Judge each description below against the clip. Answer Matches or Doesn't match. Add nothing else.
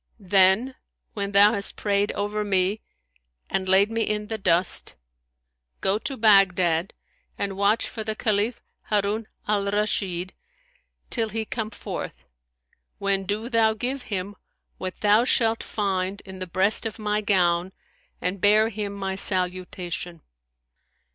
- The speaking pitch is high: Matches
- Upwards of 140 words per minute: Doesn't match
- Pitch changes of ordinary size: Doesn't match